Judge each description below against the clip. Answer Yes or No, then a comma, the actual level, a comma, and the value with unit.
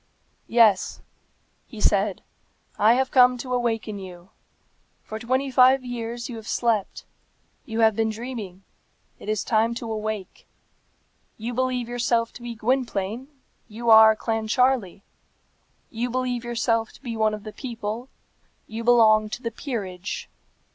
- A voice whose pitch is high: Yes, high, 230 Hz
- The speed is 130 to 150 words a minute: Yes, average, 140 wpm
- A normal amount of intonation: No, narrow, 2.2 semitones